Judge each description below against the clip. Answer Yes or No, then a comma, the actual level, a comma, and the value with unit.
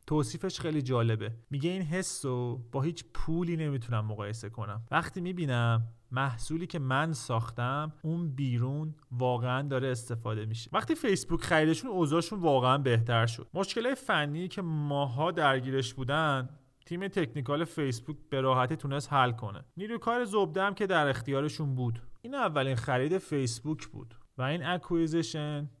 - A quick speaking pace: No, average, 145 wpm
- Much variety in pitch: No, average, 4.9 semitones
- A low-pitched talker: No, medium, 145 Hz